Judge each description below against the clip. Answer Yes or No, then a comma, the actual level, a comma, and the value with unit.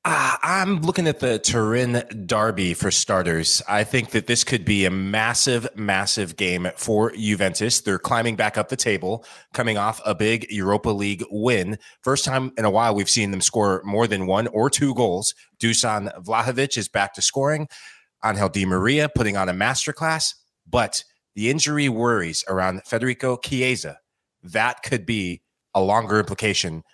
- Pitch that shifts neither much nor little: Yes, average, 4.2 semitones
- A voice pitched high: No, low, 110 Hz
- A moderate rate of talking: Yes, average, 165 wpm